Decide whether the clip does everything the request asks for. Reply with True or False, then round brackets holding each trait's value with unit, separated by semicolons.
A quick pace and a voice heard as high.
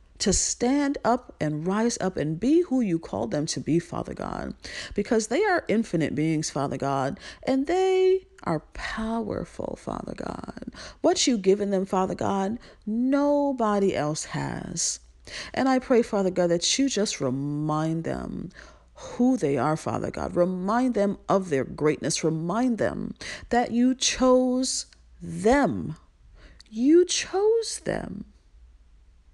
False (135 wpm; 205 Hz)